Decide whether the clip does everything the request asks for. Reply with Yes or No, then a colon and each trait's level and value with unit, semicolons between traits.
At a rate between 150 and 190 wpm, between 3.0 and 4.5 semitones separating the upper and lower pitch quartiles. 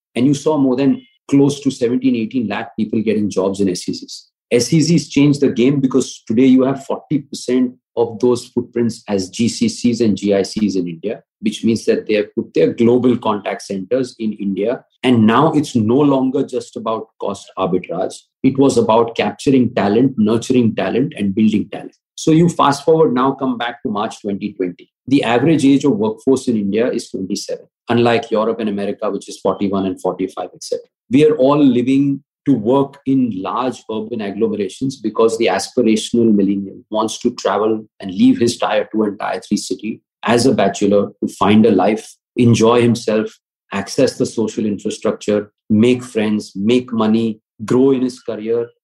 Yes: average, 170 wpm; average, 3.8 semitones